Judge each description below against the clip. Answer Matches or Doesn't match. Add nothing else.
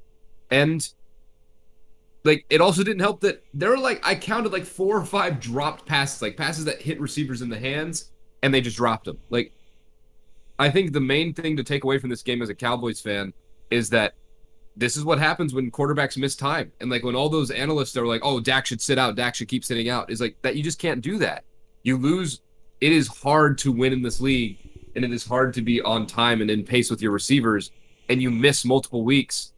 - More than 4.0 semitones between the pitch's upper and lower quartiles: Matches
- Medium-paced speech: Doesn't match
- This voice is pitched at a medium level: Doesn't match